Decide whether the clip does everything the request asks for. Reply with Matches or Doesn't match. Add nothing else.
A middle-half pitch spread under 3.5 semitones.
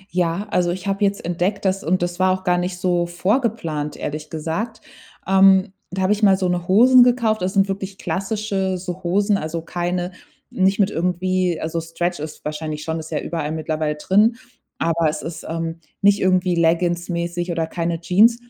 Matches